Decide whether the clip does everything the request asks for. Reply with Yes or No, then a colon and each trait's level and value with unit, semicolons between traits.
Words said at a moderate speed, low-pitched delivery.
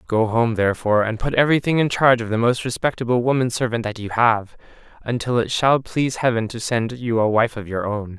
No: fast, 220 wpm; low, 115 Hz